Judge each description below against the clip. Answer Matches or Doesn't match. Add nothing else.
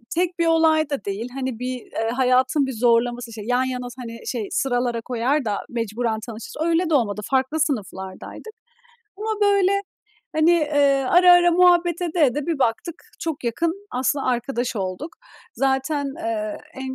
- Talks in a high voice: Matches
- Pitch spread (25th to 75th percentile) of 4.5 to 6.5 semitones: Matches